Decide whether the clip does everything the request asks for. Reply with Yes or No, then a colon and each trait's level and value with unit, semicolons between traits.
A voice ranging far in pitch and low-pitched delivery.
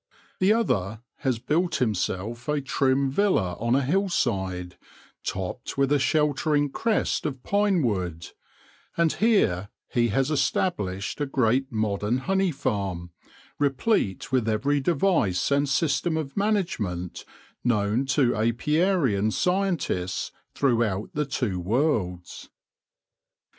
Yes: wide, 7.0 semitones; low, 130 Hz